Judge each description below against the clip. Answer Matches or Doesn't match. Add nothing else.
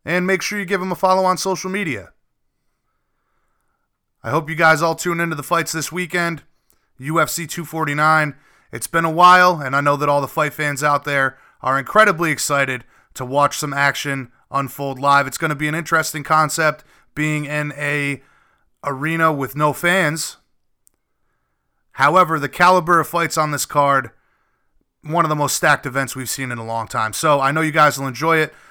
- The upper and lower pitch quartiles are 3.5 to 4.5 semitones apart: Doesn't match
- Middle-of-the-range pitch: Matches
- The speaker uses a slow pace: Doesn't match